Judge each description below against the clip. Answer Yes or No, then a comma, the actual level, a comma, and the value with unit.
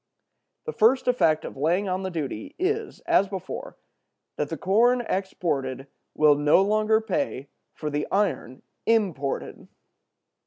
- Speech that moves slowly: Yes, slow, 130 wpm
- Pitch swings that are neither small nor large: No, wide, 7.0 semitones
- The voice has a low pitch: No, high, 190 Hz